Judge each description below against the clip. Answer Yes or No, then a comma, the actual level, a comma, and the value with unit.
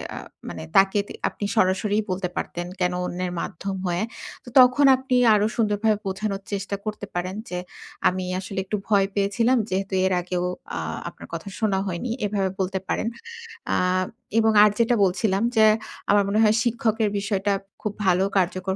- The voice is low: No, high, 200 Hz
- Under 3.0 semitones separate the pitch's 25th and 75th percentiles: Yes, narrow, 2.4 semitones